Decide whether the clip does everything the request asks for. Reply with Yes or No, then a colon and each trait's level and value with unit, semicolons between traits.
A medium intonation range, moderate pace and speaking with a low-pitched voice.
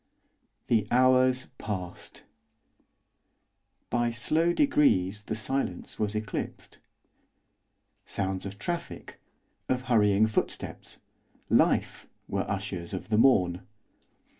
No: average, 4.6 semitones; slow, 90 wpm; low, 110 Hz